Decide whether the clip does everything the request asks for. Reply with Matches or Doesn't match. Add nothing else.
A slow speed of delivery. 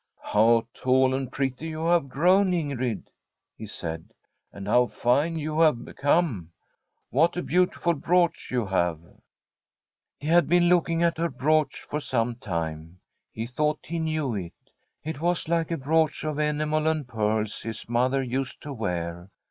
Doesn't match